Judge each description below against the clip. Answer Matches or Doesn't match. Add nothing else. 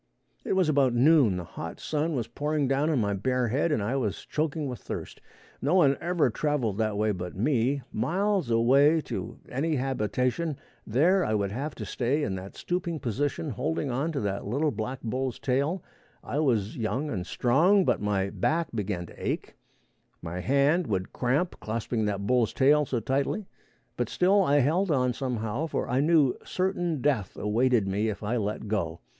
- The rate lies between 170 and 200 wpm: Matches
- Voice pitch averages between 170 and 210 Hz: Doesn't match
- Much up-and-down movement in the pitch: Matches